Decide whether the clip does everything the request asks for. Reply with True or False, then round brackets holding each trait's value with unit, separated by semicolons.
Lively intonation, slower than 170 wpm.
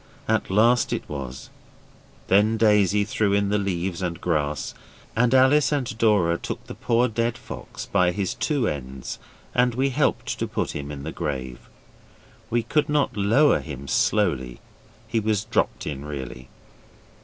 True (7.8 semitones; 155 wpm)